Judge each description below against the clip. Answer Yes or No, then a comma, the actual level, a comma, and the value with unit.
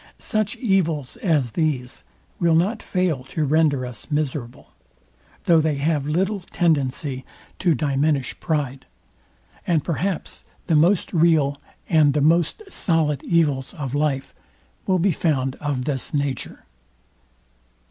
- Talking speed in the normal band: No, slow, 125 wpm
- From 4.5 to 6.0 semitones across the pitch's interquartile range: No, average, 3.4 semitones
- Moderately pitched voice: Yes, medium, 155 Hz